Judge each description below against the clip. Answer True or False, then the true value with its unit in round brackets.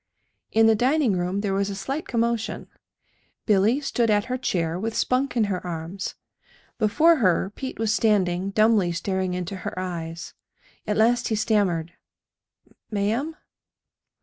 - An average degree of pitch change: True (4.0 semitones)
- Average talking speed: True (145 wpm)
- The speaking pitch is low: False (210 Hz)